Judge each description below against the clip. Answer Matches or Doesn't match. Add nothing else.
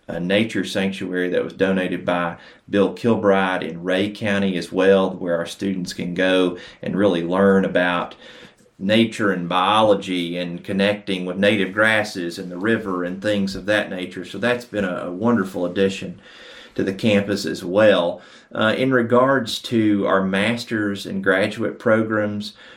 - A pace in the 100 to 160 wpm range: Matches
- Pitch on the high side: Doesn't match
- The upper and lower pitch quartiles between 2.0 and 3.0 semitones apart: Matches